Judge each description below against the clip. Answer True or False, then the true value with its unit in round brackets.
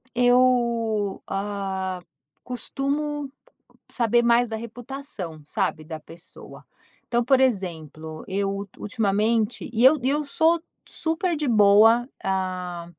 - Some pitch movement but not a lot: True (4.8 semitones)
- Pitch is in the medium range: False (225 Hz)